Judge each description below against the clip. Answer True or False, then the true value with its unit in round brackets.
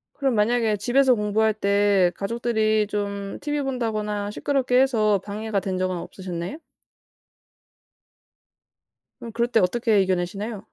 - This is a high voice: True (215 Hz)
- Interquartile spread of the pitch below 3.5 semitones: True (2.9 semitones)